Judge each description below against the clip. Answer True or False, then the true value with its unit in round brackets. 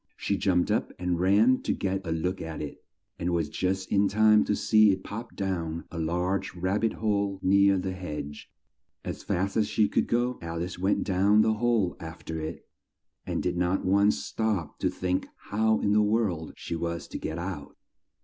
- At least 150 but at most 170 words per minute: False (195 wpm)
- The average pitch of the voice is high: False (95 Hz)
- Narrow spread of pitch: False (3.3 semitones)